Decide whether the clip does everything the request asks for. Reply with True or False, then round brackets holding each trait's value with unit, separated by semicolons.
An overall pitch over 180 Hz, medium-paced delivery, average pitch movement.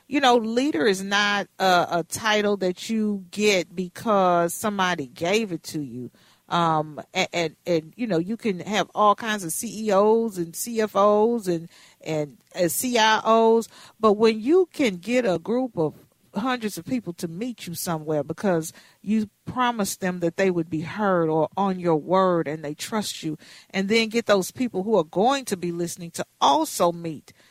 True (190 Hz; 180 wpm; 4.6 semitones)